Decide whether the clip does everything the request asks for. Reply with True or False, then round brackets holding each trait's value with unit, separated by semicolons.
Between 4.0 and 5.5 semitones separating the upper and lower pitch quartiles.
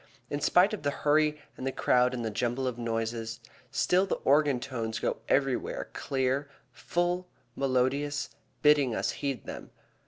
False (3.2 semitones)